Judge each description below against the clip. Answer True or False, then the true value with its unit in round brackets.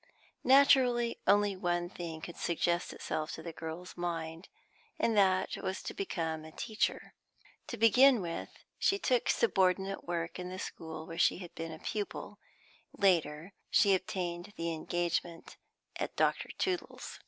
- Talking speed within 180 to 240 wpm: False (145 wpm)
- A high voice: False (175 Hz)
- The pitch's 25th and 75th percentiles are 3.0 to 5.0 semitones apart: True (3.5 semitones)